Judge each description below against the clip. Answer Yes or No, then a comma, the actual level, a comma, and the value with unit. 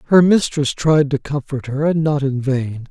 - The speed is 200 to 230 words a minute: Yes, fast, 205 wpm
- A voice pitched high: No, medium, 145 Hz